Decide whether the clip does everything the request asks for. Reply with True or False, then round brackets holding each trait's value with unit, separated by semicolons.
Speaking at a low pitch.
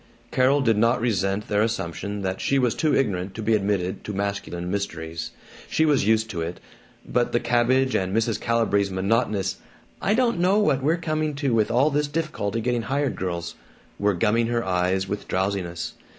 True (110 Hz)